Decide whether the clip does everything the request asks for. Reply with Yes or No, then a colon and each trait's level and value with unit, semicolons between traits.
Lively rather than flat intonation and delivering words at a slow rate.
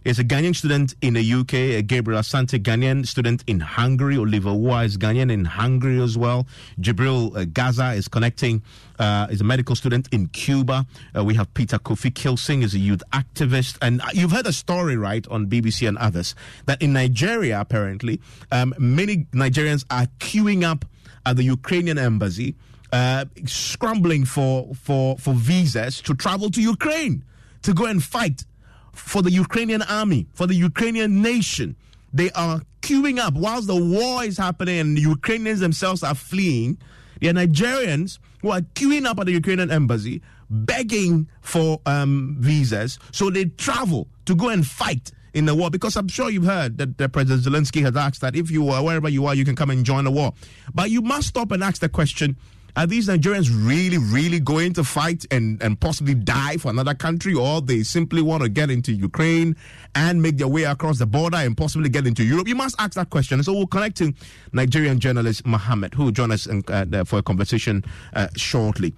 No: wide, 6.0 semitones; average, 190 wpm